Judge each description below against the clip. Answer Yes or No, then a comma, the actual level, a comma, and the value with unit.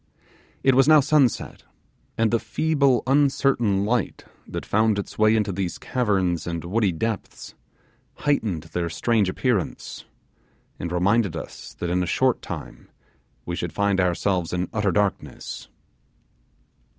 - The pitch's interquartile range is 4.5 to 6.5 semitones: Yes, wide, 5.4 semitones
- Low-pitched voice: Yes, low, 105 Hz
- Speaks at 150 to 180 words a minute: No, slow, 135 wpm